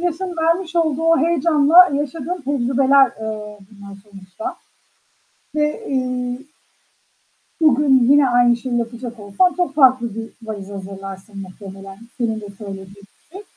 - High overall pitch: Yes, very high, 255 Hz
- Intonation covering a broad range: Yes, wide, 6.6 semitones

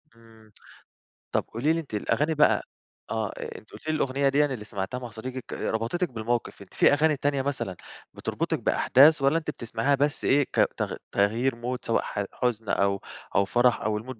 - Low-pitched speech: Yes, low, 125 Hz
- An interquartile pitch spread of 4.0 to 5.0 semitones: Yes, average, 4.3 semitones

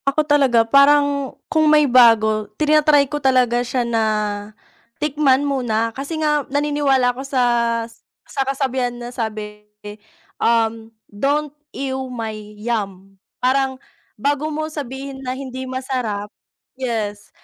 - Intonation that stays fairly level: No, average, 3.6 semitones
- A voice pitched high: Yes, very high, 260 Hz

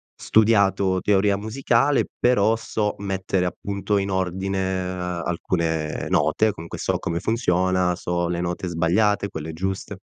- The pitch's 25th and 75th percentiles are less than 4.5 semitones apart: Yes, narrow, 2.6 semitones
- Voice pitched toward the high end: No, very low, 95 Hz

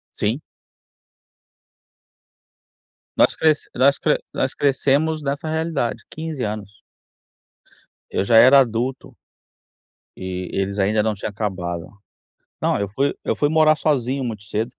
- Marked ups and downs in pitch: Yes, wide, 5.7 semitones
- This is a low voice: Yes, low, 125 Hz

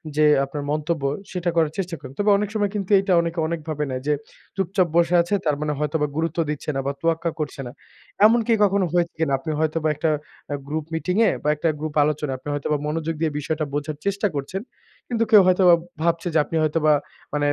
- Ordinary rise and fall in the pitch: Yes, average, 3.2 semitones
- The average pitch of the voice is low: No, medium, 160 Hz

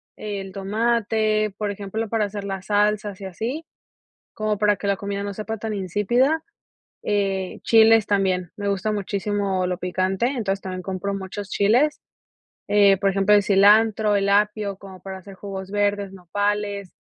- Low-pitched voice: No, high, 200 Hz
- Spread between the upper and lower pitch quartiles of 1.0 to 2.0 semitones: Yes, narrow, 1.5 semitones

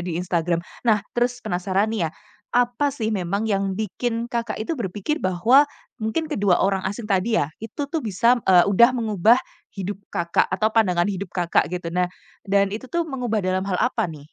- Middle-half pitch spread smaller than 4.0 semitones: No, average, 4.3 semitones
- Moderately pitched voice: No, high, 205 Hz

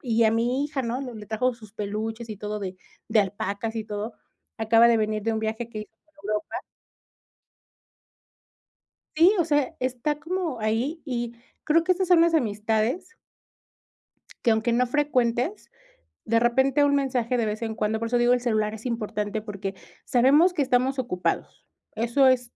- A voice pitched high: Yes, high, 235 Hz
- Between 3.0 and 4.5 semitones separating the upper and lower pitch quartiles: Yes, average, 3.5 semitones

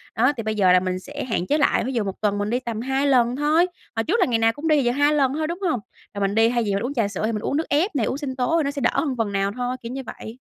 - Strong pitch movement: No, average, 4.7 semitones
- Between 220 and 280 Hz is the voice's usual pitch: Yes, very high, 250 Hz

